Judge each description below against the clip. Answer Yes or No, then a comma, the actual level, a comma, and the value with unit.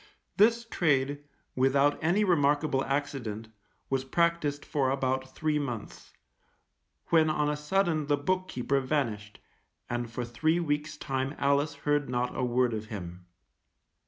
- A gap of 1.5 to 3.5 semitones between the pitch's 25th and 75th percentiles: Yes, average, 3.2 semitones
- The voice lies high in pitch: No, medium, 145 Hz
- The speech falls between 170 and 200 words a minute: No, slow, 135 wpm